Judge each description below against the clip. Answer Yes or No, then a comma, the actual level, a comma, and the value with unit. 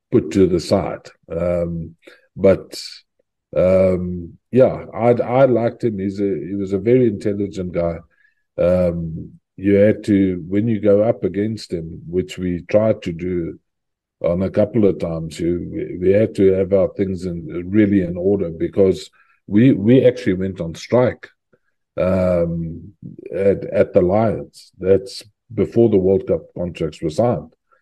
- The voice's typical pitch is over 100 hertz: No, very low, 95 Hz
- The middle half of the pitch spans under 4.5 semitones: Yes, average, 2.8 semitones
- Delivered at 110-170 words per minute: Yes, average, 150 wpm